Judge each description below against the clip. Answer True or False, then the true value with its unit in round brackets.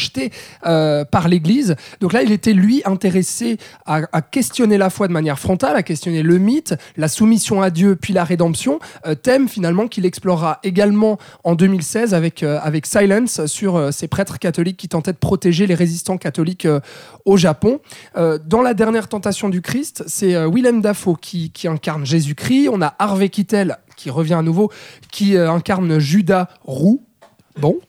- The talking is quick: False (180 wpm)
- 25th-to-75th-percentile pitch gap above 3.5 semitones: True (4.0 semitones)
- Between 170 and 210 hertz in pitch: True (185 Hz)